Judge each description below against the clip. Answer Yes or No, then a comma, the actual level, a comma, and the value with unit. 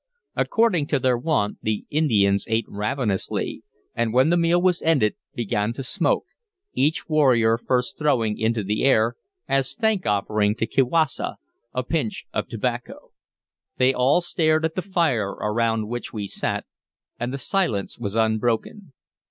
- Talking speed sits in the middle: Yes, average, 150 wpm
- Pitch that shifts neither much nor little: No, wide, 6.2 semitones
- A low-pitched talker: Yes, low, 125 Hz